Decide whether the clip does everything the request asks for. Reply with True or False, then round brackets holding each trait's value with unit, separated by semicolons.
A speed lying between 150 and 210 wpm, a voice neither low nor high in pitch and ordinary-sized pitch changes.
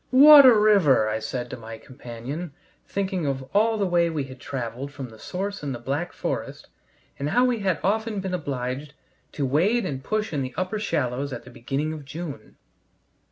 False (195 wpm; 145 Hz; 7.0 semitones)